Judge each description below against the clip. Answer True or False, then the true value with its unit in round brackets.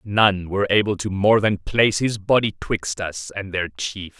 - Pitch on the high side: False (100 Hz)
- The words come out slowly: False (200 wpm)